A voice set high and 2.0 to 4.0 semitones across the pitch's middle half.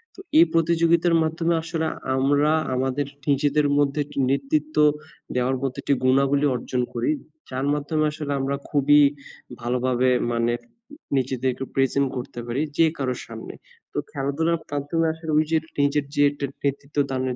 No: medium, 140 Hz; average, 2.9 semitones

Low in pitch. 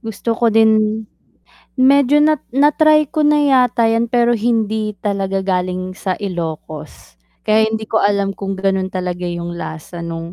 No: high, 215 Hz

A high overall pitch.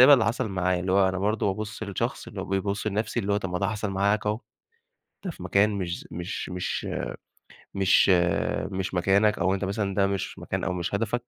No: low, 100 Hz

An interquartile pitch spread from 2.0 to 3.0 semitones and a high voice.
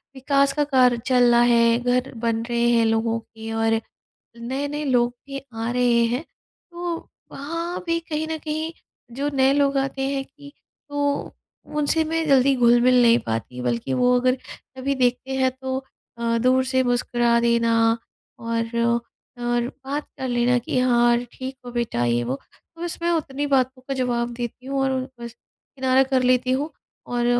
Yes: narrow, 2.6 semitones; very high, 250 Hz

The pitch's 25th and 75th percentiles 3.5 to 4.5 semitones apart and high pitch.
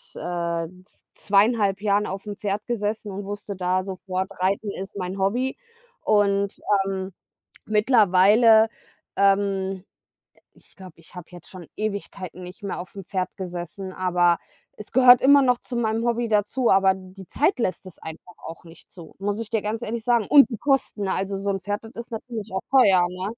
No: average, 2.8 semitones; high, 200 Hz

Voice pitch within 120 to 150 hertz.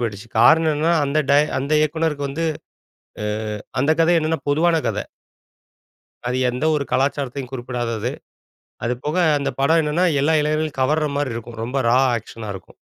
Yes: medium, 140 Hz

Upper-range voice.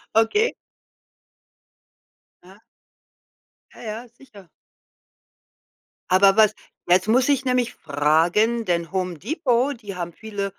Yes: high, 210 Hz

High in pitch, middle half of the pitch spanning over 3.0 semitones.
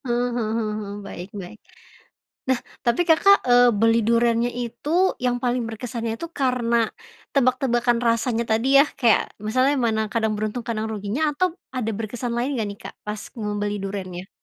No: high, 230 Hz; narrow, 2.4 semitones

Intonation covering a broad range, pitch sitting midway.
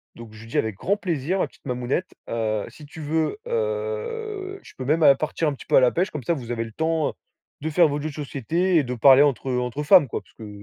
Yes: wide, 6.4 semitones; medium, 150 Hz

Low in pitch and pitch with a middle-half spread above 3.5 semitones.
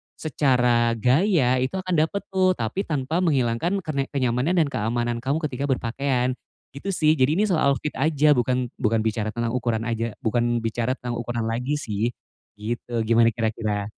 Yes: low, 125 Hz; average, 4.0 semitones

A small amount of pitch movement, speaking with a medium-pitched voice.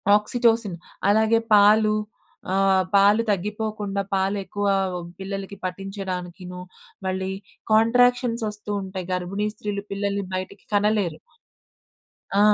No: narrow, 1.9 semitones; high, 200 Hz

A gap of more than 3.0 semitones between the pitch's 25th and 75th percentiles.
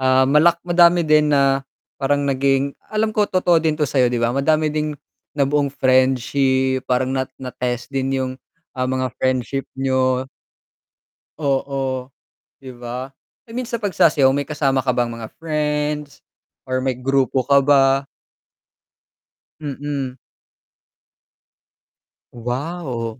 No: narrow, 2.5 semitones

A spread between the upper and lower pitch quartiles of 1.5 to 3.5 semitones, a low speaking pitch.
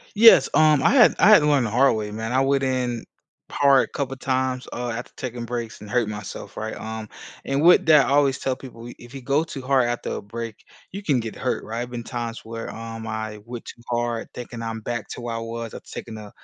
Yes: average, 2.9 semitones; low, 120 Hz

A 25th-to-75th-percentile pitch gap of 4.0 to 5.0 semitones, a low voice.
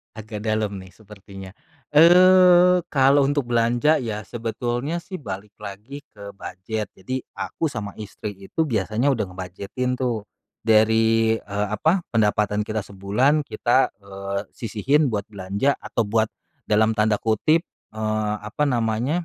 Yes: average, 4.6 semitones; low, 110 Hz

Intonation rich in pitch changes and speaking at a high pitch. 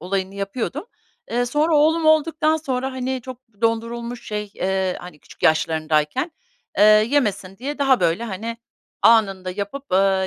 Yes: wide, 5.7 semitones; high, 230 Hz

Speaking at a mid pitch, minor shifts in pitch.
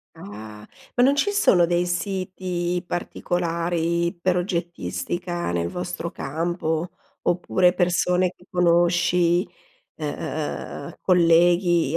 Yes: medium, 175 Hz; narrow, 1.0 semitones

